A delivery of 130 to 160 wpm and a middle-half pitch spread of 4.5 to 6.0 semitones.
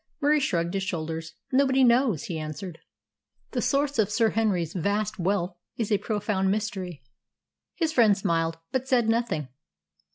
Yes: average, 150 wpm; wide, 5.6 semitones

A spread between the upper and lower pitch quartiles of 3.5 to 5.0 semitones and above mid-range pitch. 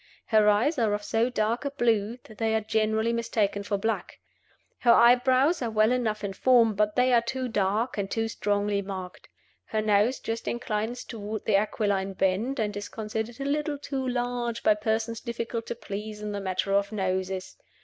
No: narrow, 2.6 semitones; high, 220 Hz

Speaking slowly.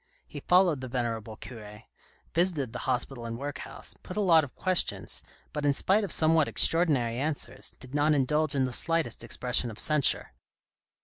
No: average, 170 wpm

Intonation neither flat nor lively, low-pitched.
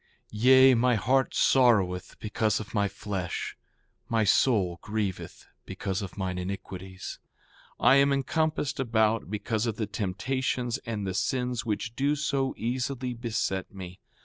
Yes: average, 4.6 semitones; low, 110 Hz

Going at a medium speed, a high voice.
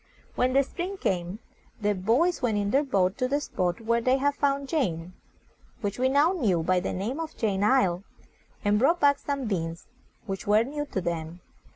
Yes: average, 195 wpm; high, 225 Hz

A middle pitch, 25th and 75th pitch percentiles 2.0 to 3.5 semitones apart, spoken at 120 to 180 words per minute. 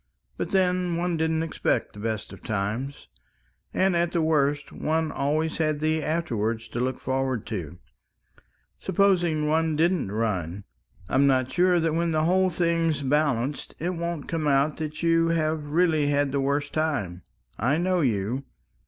No: medium, 155 Hz; average, 4.1 semitones; average, 160 wpm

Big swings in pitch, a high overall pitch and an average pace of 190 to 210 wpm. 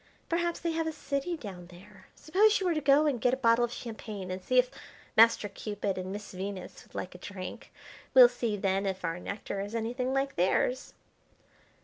Yes: wide, 5.9 semitones; high, 225 Hz; fast, 205 wpm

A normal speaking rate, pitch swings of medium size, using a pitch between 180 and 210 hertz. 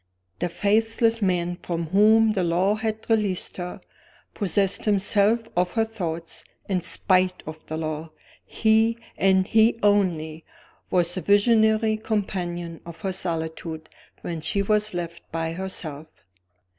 No: slow, 130 wpm; average, 4.1 semitones; high, 190 Hz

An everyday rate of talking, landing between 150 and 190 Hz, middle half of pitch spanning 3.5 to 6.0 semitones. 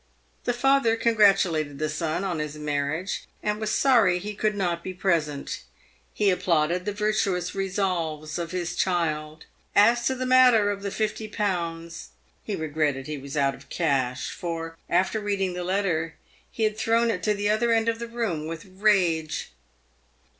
Yes: average, 165 wpm; medium, 185 Hz; average, 5.0 semitones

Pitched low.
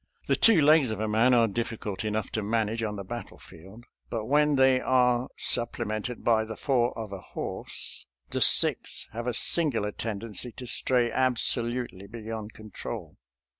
Yes: low, 115 Hz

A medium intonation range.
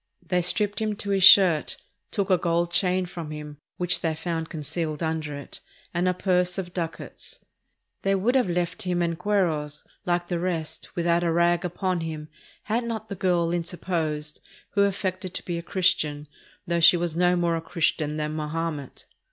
No: narrow, 2.3 semitones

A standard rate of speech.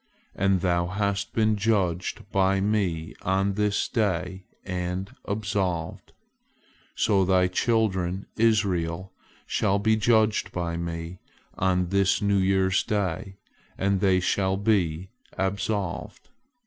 No: slow, 110 wpm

